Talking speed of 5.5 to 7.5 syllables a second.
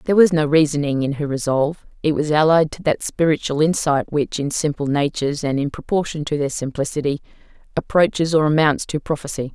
Yes: 5.8 syllables/s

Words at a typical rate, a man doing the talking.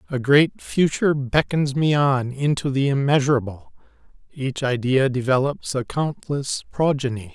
No: slow, 120 wpm; male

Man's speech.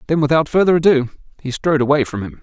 Yes: male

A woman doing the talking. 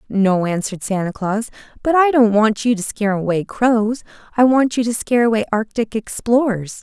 Yes: female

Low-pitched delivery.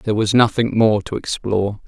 Yes: low, 105 Hz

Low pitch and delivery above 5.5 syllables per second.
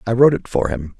Yes: low, 110 Hz; 6.9 syllables/s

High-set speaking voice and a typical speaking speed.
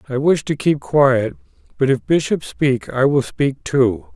No: medium, 140 Hz; average, 190 wpm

